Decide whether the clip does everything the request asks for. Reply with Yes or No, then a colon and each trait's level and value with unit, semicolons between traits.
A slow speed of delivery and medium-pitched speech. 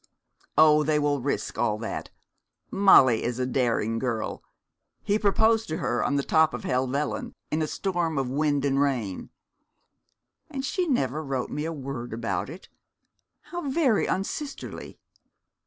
No: average, 150 wpm; medium, 145 Hz